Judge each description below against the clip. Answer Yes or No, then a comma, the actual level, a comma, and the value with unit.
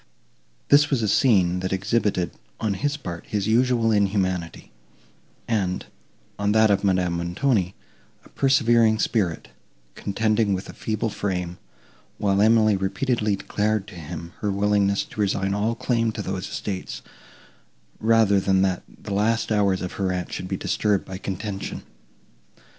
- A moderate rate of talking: Yes, average, 145 wpm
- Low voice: Yes, low, 100 Hz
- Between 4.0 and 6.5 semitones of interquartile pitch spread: No, average, 2.8 semitones